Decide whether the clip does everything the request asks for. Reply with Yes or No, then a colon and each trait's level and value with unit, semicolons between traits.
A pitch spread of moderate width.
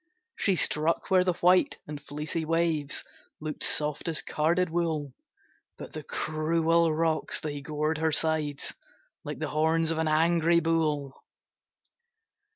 No: narrow, 1.6 semitones